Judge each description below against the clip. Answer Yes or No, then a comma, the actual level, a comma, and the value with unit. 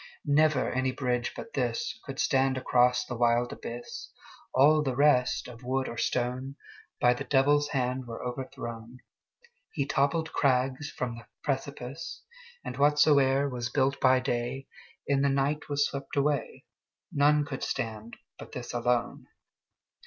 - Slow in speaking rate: Yes, slow, 125 wpm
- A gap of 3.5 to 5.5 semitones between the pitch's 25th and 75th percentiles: No, narrow, 2.6 semitones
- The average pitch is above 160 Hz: No, low, 135 Hz